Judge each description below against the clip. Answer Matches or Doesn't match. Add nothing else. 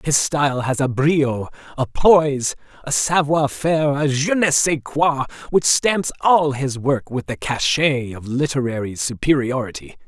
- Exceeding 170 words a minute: Doesn't match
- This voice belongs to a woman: Doesn't match